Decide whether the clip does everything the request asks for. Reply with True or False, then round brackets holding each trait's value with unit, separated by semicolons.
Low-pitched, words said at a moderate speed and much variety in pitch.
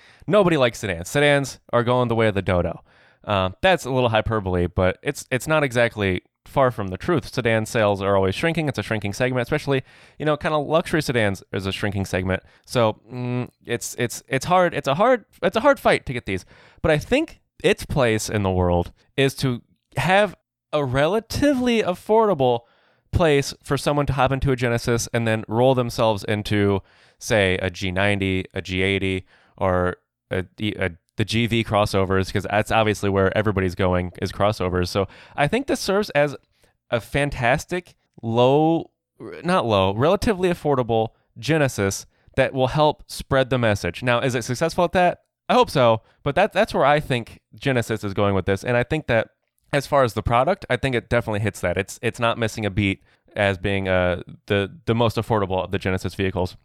True (115 Hz; 190 wpm; 6.2 semitones)